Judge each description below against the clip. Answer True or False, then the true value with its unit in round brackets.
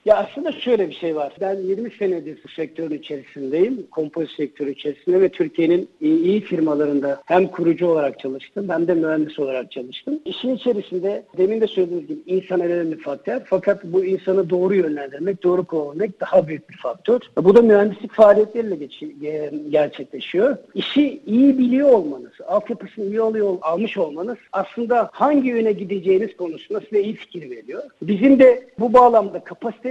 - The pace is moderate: False (155 wpm)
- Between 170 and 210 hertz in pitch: True (190 Hz)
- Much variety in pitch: True (6.4 semitones)